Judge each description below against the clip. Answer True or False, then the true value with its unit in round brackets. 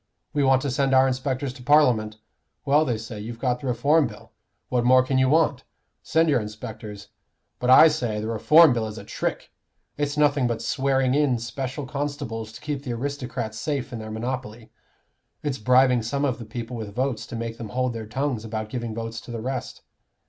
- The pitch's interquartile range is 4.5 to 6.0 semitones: False (3.4 semitones)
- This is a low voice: True (125 Hz)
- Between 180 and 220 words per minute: True (200 wpm)